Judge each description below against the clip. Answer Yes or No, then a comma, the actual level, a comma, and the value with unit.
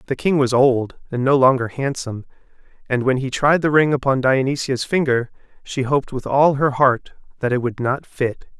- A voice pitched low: Yes, low, 130 Hz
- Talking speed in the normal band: Yes, average, 195 wpm